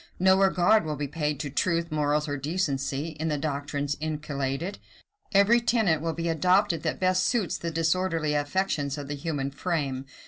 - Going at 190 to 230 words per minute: No, average, 170 wpm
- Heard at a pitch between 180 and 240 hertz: No, medium, 155 Hz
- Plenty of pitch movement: No, average, 4.1 semitones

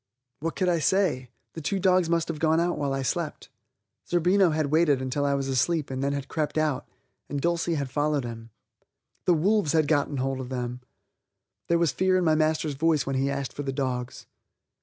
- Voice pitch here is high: No, medium, 150 Hz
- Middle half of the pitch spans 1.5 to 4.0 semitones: Yes, average, 3.7 semitones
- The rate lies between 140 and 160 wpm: No, fast, 205 wpm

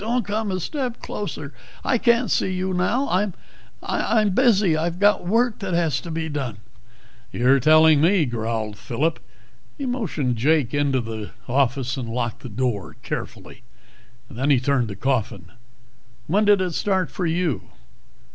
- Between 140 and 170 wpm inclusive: Yes, average, 160 wpm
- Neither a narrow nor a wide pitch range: No, wide, 7.9 semitones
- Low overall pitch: No, medium, 155 Hz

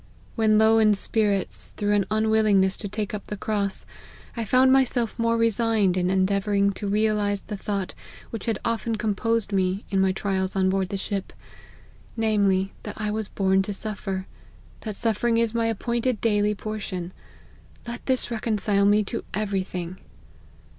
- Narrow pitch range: Yes, narrow, 2.3 semitones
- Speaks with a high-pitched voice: Yes, high, 210 Hz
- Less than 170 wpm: Yes, average, 160 wpm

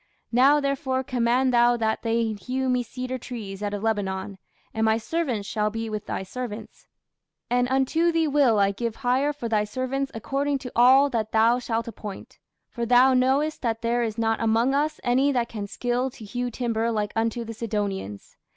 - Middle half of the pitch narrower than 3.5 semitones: Yes, average, 2.9 semitones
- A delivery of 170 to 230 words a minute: Yes, average, 190 wpm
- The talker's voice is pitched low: No, high, 235 Hz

